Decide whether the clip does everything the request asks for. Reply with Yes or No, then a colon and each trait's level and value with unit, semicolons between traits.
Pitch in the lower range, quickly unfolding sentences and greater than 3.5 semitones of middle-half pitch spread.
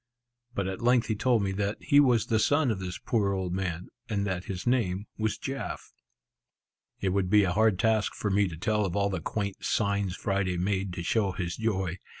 No: low, 100 Hz; fast, 210 wpm; average, 2.8 semitones